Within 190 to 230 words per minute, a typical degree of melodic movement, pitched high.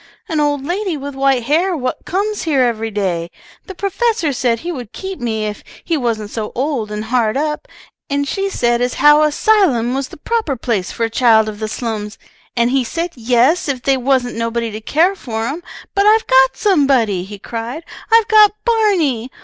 No: average, 200 wpm; wide, 6.4 semitones; very high, 265 Hz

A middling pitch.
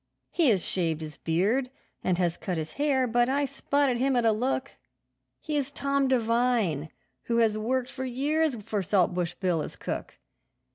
No: high, 240 Hz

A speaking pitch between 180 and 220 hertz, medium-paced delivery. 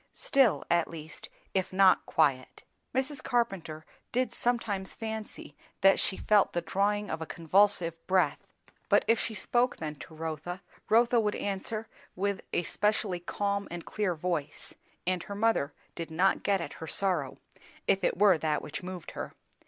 Yes: high, 190 Hz; average, 160 wpm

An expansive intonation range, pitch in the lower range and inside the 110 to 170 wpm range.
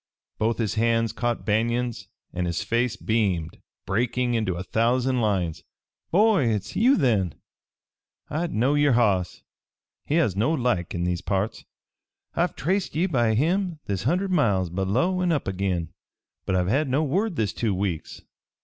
Yes: wide, 7.0 semitones; low, 115 Hz; average, 160 wpm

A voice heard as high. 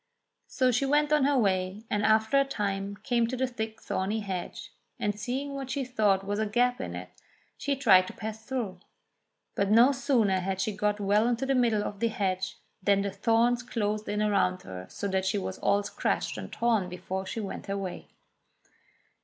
Yes: high, 210 Hz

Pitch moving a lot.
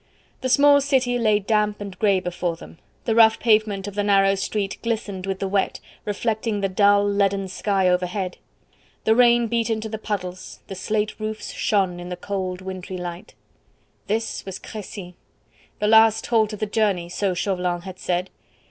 No: average, 2.8 semitones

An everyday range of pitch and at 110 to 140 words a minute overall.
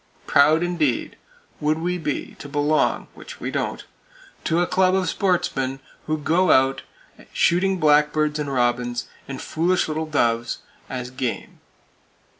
Yes: average, 4.2 semitones; slow, 135 wpm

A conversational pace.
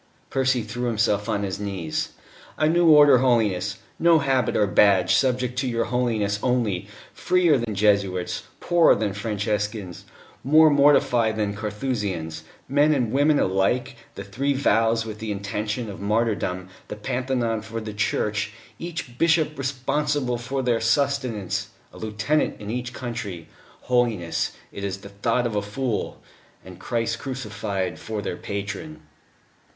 Yes: average, 145 wpm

